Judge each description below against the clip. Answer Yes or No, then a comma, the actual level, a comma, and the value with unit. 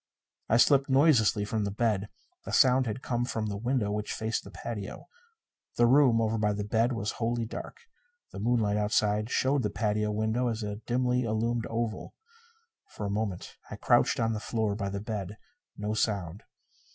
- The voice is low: Yes, low, 110 Hz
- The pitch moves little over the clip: Yes, narrow, 2.3 semitones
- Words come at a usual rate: Yes, average, 180 wpm